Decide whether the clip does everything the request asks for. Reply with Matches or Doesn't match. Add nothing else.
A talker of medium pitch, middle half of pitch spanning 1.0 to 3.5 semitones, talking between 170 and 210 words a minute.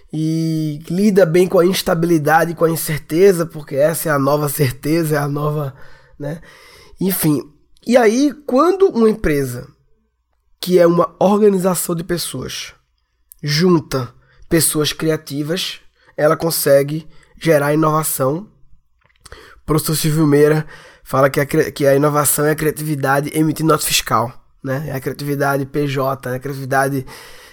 Doesn't match